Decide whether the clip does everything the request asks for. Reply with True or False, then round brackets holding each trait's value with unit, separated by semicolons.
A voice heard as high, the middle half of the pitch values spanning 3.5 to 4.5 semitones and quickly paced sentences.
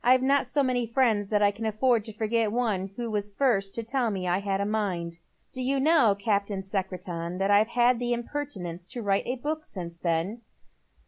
True (215 Hz; 4.0 semitones; 220 wpm)